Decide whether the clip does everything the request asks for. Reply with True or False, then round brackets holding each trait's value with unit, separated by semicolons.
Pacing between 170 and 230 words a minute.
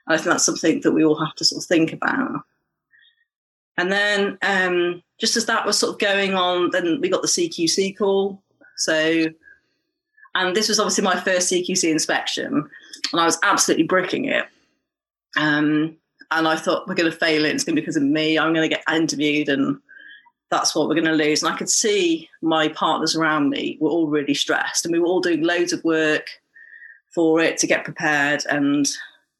True (205 wpm)